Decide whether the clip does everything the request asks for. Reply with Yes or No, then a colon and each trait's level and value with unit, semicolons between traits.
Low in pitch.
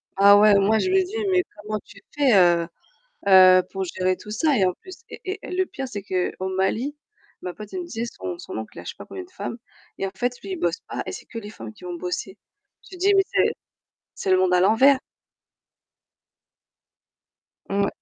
No: high, 210 Hz